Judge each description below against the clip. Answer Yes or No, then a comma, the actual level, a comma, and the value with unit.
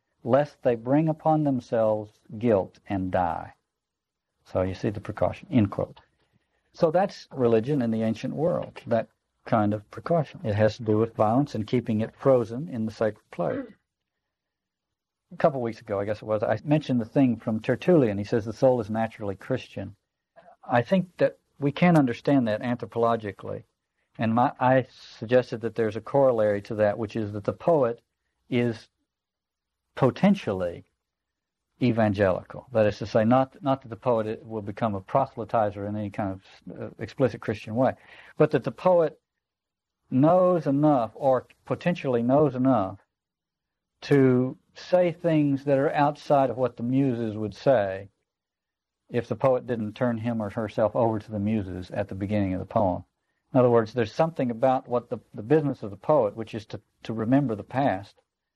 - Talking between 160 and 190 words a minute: Yes, average, 170 wpm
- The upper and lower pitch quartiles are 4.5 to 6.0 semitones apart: No, average, 3.8 semitones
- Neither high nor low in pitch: No, low, 115 Hz